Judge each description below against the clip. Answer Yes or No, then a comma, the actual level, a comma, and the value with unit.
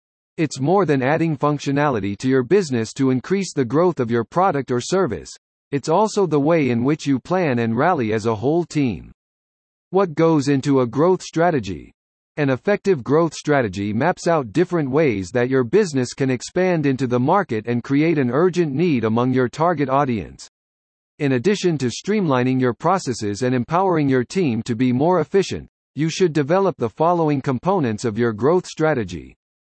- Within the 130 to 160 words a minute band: No, average, 175 wpm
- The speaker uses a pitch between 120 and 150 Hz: Yes, medium, 140 Hz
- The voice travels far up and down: Yes, wide, 5.9 semitones